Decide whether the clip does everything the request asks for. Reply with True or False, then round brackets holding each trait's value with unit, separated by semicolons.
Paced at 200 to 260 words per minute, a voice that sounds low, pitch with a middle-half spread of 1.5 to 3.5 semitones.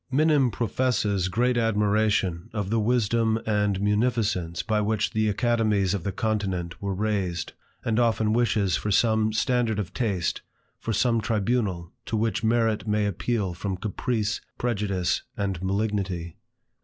False (140 wpm; 105 Hz; 2.7 semitones)